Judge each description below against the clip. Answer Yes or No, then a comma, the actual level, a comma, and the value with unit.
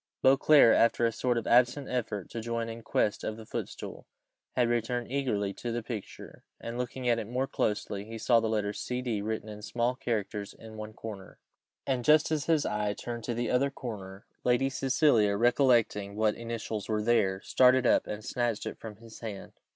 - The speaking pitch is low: Yes, low, 115 Hz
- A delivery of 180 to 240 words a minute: Yes, average, 190 wpm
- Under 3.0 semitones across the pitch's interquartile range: Yes, narrow, 2.6 semitones